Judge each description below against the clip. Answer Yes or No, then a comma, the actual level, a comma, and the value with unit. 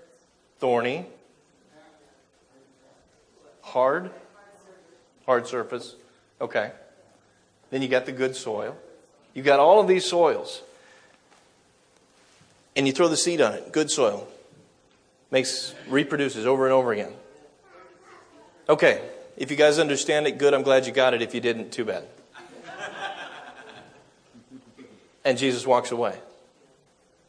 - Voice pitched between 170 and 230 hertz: No, medium, 140 Hz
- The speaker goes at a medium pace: No, slow, 115 wpm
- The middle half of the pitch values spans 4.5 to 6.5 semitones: Yes, average, 5.1 semitones